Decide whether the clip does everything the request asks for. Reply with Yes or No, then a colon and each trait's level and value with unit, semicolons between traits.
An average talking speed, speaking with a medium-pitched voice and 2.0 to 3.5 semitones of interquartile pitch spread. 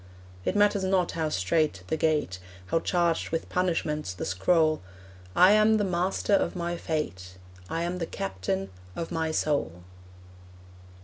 No: average, 145 wpm; medium, 165 Hz; average, 4.1 semitones